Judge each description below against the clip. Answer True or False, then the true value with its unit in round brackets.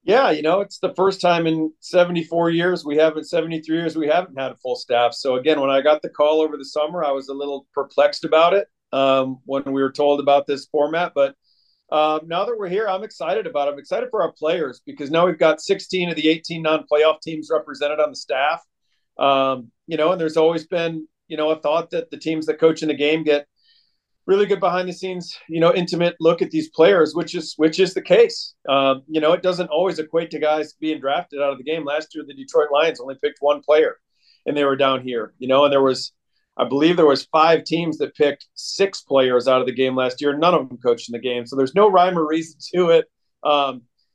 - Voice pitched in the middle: True (155 Hz)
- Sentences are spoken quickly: True (240 wpm)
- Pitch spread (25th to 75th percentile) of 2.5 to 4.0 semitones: True (3.4 semitones)